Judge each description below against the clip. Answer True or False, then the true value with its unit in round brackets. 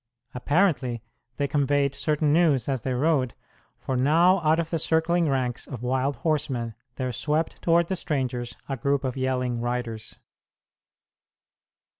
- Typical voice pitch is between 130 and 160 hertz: True (140 Hz)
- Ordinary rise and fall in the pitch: True (3.9 semitones)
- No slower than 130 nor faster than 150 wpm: True (140 wpm)